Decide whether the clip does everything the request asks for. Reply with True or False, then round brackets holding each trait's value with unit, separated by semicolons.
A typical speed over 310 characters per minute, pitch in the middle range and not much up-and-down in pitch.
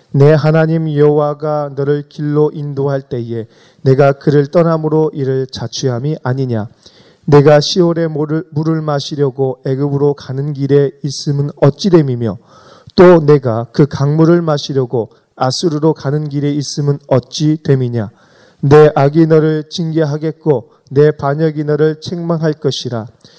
False (280 characters per minute; 145 Hz; 2.2 semitones)